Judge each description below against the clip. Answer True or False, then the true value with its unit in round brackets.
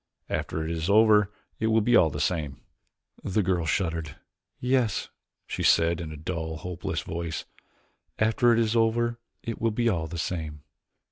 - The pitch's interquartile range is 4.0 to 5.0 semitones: False (5.6 semitones)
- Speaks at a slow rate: False (165 wpm)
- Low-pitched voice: True (90 Hz)